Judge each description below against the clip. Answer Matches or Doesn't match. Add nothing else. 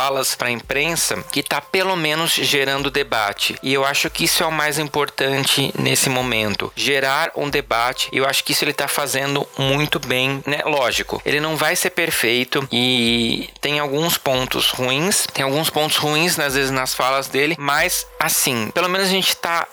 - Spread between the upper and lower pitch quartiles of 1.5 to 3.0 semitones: Matches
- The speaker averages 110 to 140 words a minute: Doesn't match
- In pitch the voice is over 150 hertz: Doesn't match